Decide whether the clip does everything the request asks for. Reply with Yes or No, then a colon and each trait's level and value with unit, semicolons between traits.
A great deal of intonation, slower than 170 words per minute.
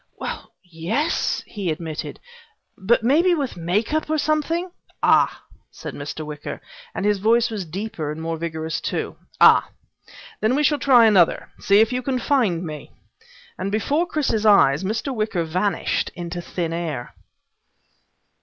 Yes: wide, 7.3 semitones; average, 155 wpm